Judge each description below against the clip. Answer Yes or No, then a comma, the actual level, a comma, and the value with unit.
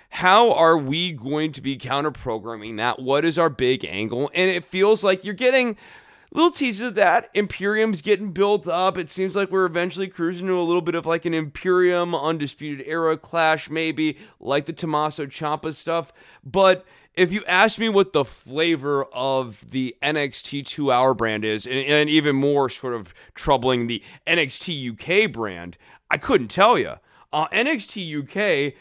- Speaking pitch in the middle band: Yes, medium, 160 Hz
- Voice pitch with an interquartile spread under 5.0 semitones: No, average, 5.3 semitones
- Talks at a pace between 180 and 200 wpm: No, average, 170 wpm